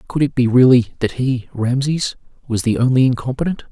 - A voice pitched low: Yes, low, 125 Hz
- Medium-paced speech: Yes, average, 180 wpm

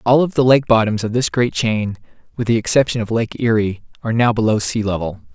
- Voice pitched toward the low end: Yes, low, 115 Hz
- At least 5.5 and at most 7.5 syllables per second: Yes, 5.9 syllables/s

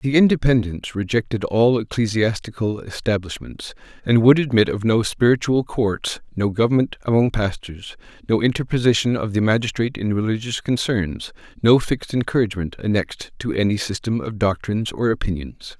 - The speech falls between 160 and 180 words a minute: No, slow, 135 wpm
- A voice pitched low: Yes, low, 110 Hz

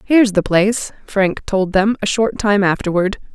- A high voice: Yes, high, 200 Hz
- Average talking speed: Yes, average, 180 wpm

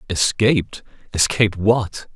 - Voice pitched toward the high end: No, low, 105 Hz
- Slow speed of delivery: Yes, slow, 85 wpm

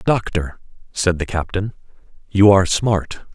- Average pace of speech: No, slow, 125 wpm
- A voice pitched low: Yes, very low, 95 Hz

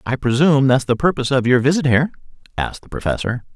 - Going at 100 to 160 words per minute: No, average, 200 wpm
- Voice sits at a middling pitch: No, low, 130 Hz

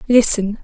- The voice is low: No, high, 220 Hz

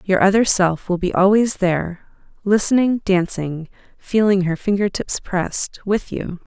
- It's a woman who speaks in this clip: Yes, female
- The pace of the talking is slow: Yes, slow, 130 wpm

